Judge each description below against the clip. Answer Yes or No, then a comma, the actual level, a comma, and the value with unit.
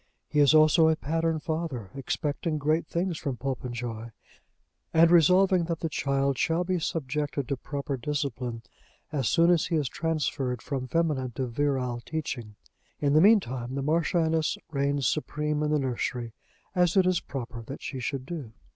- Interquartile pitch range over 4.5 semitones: No, average, 3.8 semitones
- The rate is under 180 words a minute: Yes, average, 165 wpm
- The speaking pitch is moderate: Yes, medium, 145 Hz